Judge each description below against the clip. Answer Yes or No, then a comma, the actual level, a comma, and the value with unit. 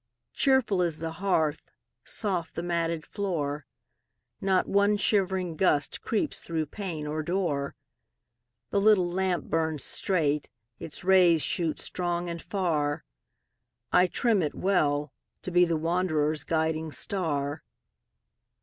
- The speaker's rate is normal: No, slow, 120 wpm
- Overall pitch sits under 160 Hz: No, medium, 170 Hz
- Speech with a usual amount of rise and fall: Yes, average, 3.4 semitones